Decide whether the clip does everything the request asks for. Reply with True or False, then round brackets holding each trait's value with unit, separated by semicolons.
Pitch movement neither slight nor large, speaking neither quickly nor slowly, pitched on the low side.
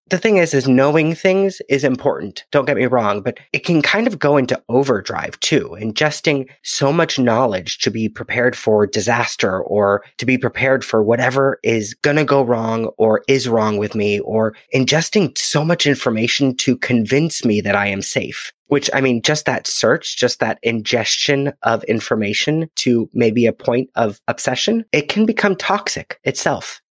True (4.6 semitones; 180 wpm; 130 Hz)